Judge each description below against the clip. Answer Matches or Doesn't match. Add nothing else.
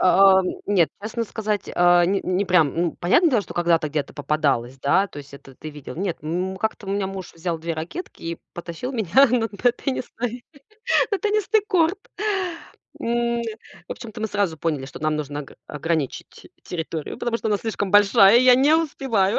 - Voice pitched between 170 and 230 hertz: Matches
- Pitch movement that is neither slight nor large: Doesn't match